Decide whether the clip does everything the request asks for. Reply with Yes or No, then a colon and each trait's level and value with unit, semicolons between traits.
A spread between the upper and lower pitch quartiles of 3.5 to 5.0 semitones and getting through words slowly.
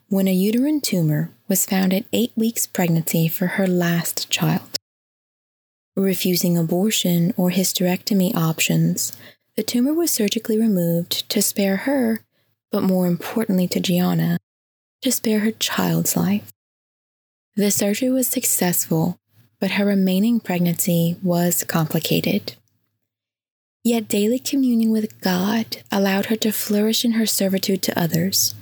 Yes: average, 4.2 semitones; slow, 130 wpm